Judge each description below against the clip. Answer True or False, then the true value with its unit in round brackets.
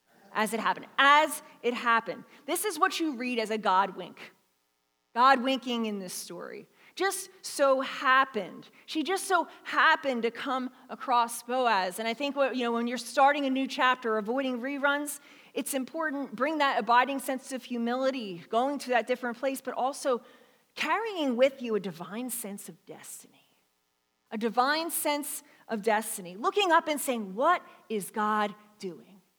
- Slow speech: False (165 wpm)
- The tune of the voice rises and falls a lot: False (4.2 semitones)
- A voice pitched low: False (255 Hz)